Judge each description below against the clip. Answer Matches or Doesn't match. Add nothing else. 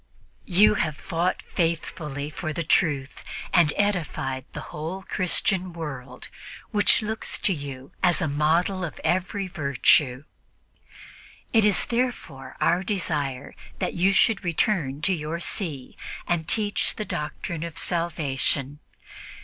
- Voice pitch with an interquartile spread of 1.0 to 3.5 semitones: Doesn't match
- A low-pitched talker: Doesn't match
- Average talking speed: Doesn't match